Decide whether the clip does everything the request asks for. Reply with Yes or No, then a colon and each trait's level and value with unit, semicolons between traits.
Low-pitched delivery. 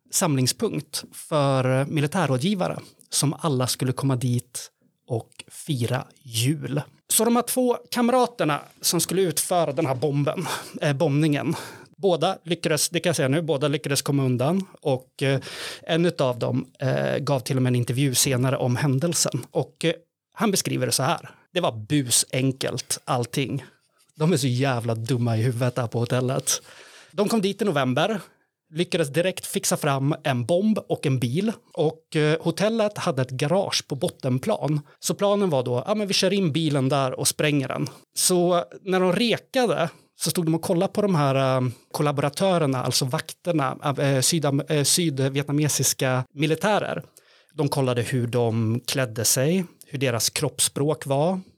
No: medium, 150 Hz